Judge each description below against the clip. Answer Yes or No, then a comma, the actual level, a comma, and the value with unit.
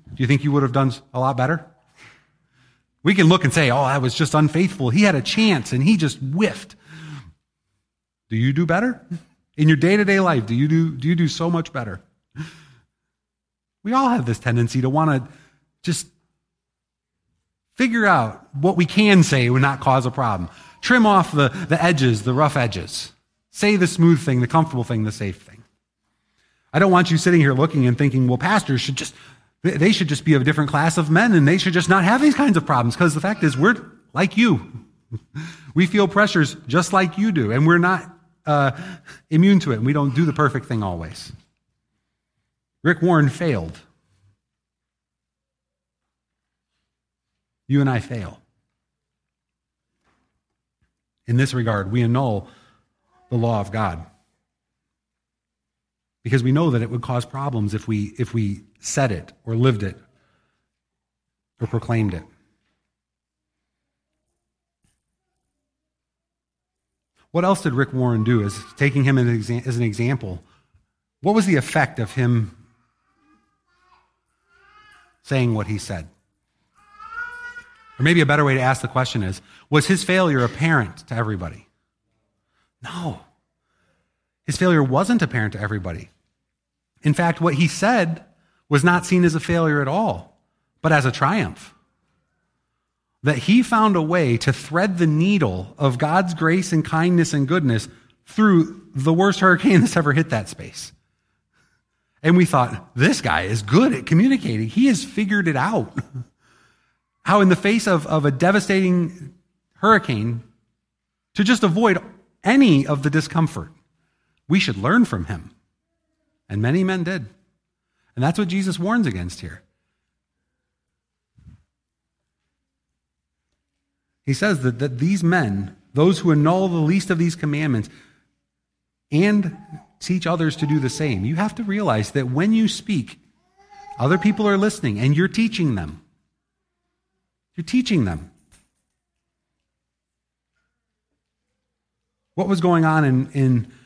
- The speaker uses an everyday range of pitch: No, wide, 7.6 semitones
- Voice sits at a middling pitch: Yes, medium, 145 Hz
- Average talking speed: Yes, average, 150 wpm